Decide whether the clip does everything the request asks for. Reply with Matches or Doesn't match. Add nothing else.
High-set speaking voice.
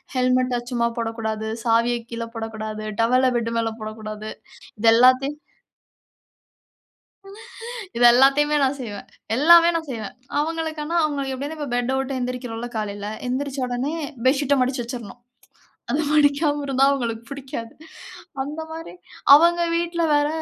Matches